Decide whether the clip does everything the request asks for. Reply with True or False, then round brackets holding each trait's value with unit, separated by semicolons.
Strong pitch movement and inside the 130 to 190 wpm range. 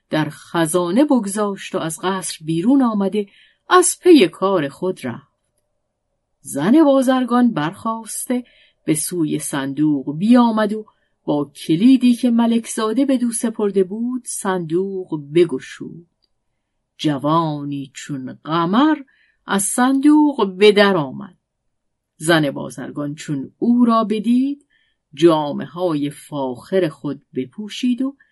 False (8.5 semitones; 110 wpm)